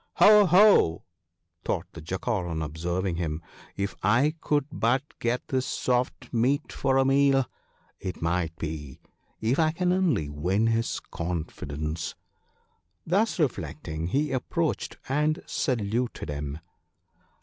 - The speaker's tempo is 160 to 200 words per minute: No, average, 140 wpm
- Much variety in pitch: Yes, wide, 8.8 semitones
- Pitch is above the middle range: No, low, 110 Hz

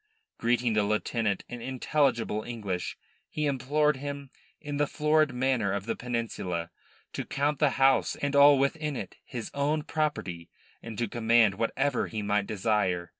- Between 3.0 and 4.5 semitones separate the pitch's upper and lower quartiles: No, average, 5.0 semitones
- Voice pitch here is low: Yes, low, 120 Hz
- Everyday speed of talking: Yes, average, 155 wpm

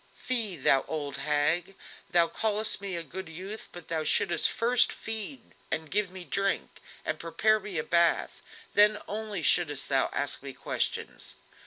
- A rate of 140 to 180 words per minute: Yes, average, 160 wpm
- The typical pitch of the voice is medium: Yes, medium, 180 Hz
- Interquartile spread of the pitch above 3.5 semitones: Yes, average, 4.8 semitones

